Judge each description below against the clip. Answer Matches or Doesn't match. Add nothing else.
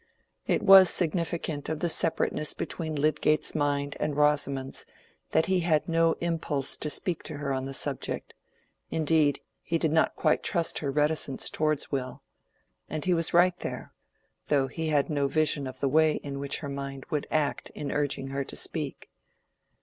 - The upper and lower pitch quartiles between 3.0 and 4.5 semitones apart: Doesn't match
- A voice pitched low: Doesn't match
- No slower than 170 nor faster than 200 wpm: Matches